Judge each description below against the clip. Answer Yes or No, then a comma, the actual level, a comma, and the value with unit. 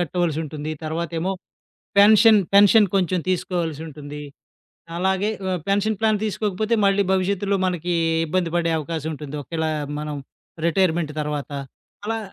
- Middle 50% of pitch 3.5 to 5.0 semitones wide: Yes, average, 3.9 semitones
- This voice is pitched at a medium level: Yes, medium, 175 Hz